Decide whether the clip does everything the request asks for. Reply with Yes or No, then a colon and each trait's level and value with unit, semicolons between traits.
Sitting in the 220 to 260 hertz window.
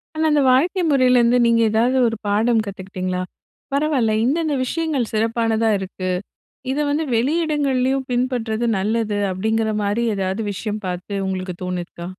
Yes: high, 230 Hz